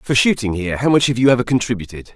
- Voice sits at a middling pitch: No, low, 120 Hz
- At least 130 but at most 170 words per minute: No, fast, 250 wpm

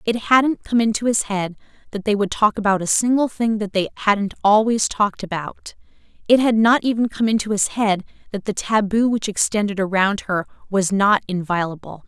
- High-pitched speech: Yes, high, 210 Hz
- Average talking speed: Yes, average, 190 wpm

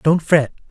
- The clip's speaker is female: No, male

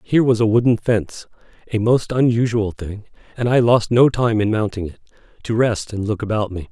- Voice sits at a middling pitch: No, low, 110 Hz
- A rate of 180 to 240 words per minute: Yes, average, 190 wpm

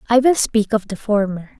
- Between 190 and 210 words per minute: No, fast, 225 wpm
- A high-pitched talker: Yes, high, 215 Hz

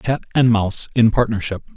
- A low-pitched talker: Yes, low, 110 Hz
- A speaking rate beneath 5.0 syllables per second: No, 5.6 syllables/s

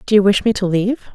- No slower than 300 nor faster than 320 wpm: Yes, fast, 315 wpm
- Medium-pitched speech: No, high, 205 Hz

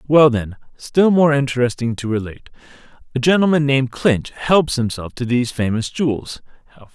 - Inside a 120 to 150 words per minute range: Yes, average, 145 wpm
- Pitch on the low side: Yes, low, 130 Hz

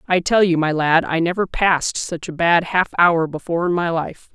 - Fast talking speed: Yes, fast, 235 wpm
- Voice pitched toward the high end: No, medium, 170 Hz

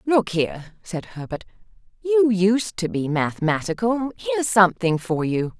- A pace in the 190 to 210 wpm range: No, average, 140 wpm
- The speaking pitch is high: Yes, high, 200 Hz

